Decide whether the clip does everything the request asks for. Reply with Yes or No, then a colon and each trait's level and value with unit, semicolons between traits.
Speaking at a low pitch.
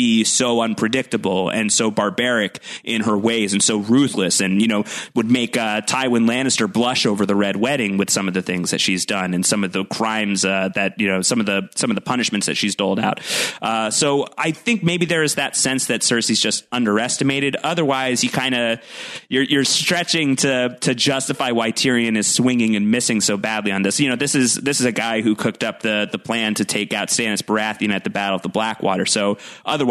Yes: low, 115 Hz